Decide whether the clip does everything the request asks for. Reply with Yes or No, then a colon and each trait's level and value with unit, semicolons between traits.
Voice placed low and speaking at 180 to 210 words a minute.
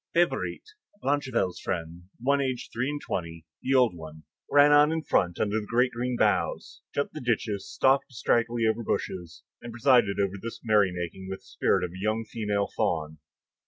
Yes: low, 110 Hz; average, 185 wpm